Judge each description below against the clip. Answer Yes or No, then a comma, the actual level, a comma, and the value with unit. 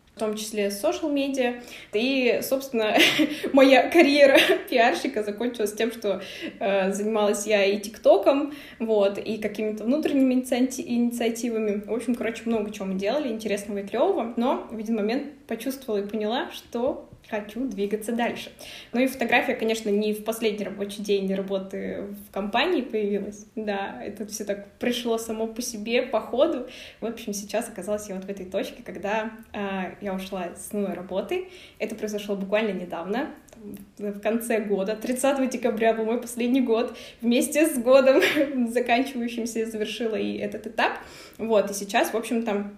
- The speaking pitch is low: No, high, 220 Hz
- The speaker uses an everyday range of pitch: Yes, average, 3.4 semitones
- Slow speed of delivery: No, average, 155 wpm